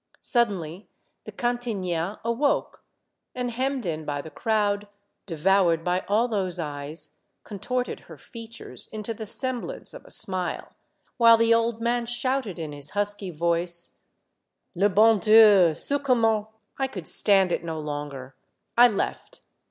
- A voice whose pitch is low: No, high, 205 Hz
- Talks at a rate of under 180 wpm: Yes, average, 155 wpm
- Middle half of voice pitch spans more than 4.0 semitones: Yes, average, 5.3 semitones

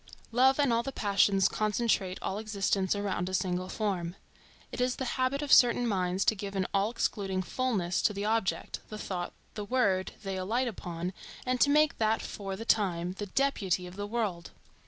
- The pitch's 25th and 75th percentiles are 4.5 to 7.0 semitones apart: No, average, 4.0 semitones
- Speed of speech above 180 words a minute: Yes, average, 190 wpm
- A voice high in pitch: Yes, high, 205 Hz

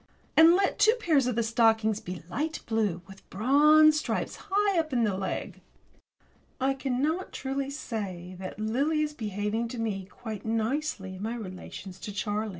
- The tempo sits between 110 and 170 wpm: Yes, average, 160 wpm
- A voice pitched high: Yes, high, 230 Hz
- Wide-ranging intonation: Yes, wide, 6.3 semitones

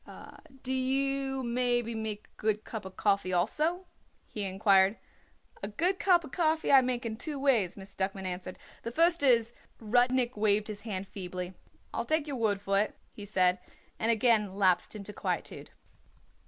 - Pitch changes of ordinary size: Yes, average, 4.9 semitones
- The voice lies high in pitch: Yes, high, 220 Hz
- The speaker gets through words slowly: No, average, 165 wpm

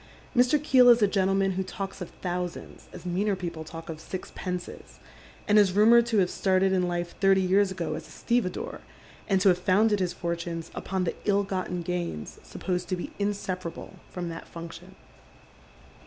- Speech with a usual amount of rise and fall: No, narrow, 2.3 semitones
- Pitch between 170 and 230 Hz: Yes, medium, 185 Hz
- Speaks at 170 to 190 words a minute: Yes, average, 175 wpm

